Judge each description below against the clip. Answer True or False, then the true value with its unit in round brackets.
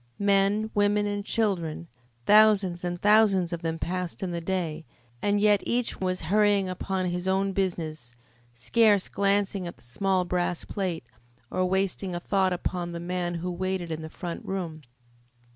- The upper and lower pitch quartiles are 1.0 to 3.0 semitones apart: True (2.6 semitones)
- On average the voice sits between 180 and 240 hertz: True (185 Hz)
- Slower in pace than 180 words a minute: True (165 wpm)